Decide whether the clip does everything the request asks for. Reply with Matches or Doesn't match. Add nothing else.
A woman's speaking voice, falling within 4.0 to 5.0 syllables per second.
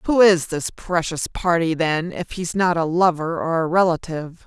Matches